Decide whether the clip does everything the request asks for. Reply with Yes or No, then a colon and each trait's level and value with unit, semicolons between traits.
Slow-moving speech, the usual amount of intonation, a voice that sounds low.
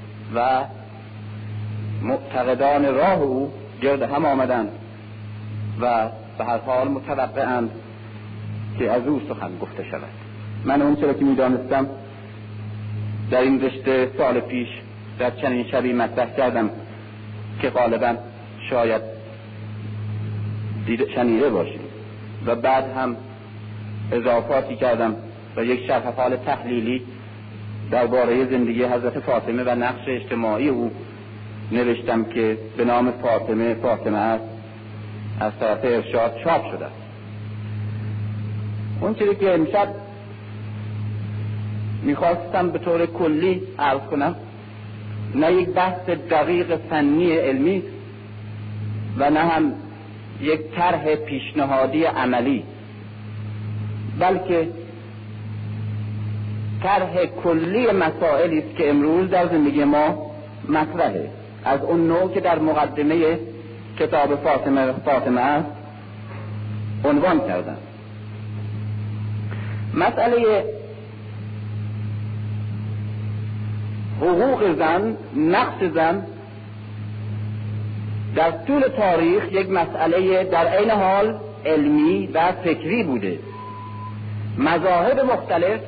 Yes: slow, 95 wpm; average, 4.7 semitones; low, 110 Hz